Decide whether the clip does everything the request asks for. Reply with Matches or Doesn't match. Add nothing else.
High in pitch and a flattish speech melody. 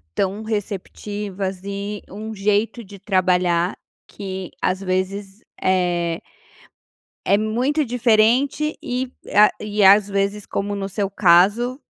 Matches